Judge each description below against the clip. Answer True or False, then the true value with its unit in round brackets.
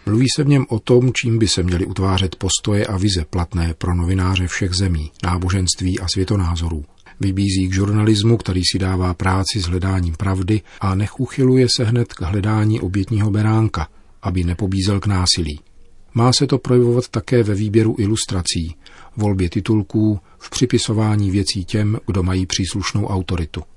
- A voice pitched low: True (100 Hz)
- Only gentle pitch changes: False (3.1 semitones)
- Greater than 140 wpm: True (160 wpm)